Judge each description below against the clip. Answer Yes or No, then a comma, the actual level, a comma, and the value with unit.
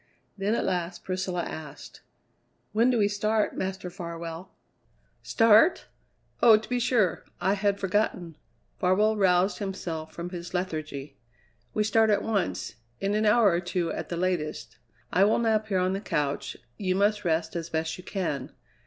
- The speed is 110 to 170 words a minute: Yes, average, 160 wpm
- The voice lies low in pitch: No, medium, 185 Hz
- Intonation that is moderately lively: Yes, average, 3.6 semitones